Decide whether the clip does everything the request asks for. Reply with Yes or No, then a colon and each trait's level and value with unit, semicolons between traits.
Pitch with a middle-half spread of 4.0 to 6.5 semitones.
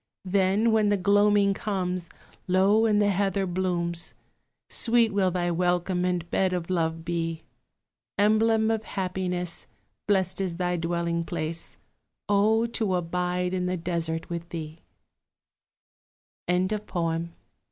No: average, 2.8 semitones